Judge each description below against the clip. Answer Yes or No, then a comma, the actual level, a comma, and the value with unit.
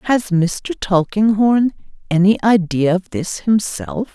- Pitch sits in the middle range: No, high, 200 Hz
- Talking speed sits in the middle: No, slow, 115 wpm